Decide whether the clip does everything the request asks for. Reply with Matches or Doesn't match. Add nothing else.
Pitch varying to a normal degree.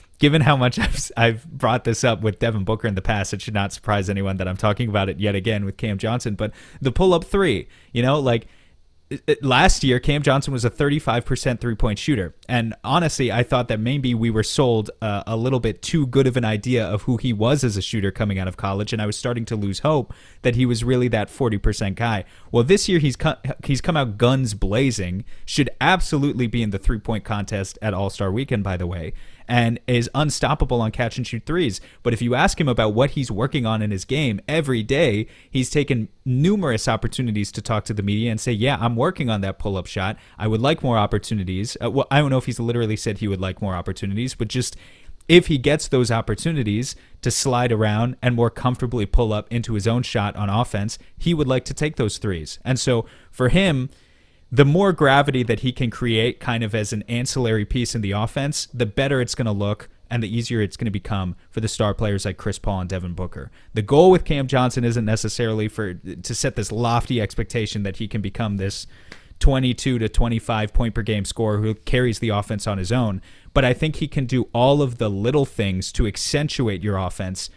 Matches